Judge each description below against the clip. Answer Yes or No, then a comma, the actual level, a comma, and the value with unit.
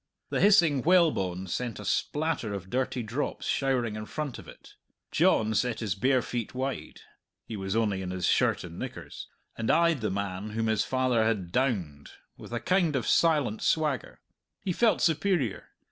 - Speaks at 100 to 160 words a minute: No, average, 175 wpm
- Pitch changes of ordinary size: No, wide, 6.1 semitones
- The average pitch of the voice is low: Yes, low, 120 Hz